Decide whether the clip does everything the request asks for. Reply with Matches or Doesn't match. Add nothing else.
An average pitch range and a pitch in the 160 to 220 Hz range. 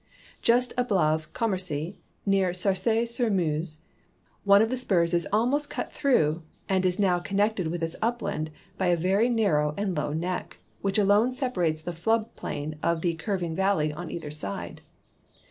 Matches